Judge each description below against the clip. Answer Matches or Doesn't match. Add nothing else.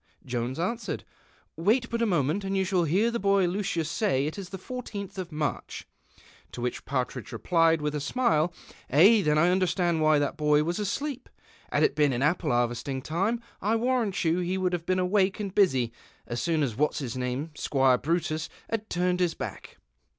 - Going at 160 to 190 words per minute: Doesn't match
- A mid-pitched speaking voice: Matches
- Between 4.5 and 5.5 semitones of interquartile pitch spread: Matches